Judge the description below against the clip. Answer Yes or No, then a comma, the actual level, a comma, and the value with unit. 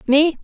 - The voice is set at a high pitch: Yes, very high, 300 Hz